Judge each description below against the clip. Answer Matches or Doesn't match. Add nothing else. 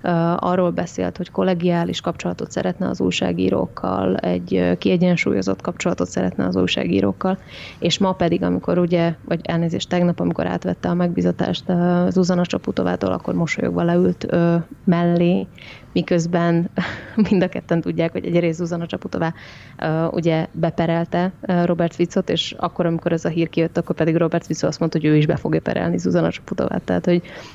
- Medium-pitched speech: Matches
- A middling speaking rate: Doesn't match